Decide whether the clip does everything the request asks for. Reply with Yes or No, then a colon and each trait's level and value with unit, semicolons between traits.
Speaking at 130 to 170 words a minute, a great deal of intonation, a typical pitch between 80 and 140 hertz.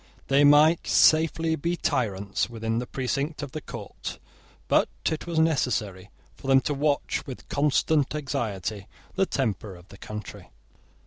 Yes: average, 145 wpm; wide, 5.8 semitones; low, 135 Hz